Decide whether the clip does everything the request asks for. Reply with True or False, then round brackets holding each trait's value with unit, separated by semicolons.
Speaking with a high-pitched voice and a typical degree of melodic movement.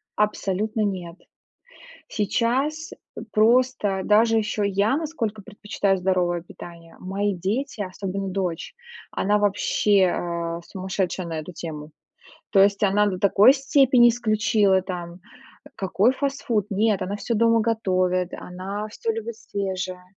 True (200 Hz; 3.3 semitones)